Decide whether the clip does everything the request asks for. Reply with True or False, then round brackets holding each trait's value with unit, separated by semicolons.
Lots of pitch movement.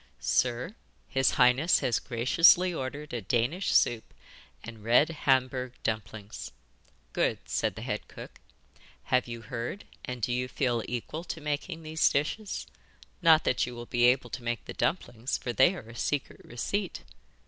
False (4.4 semitones)